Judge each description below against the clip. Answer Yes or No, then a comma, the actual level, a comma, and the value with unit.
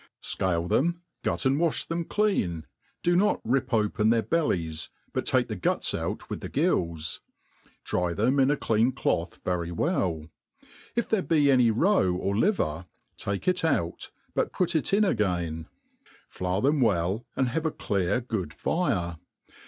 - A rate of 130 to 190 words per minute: Yes, average, 160 wpm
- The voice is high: No, low, 115 Hz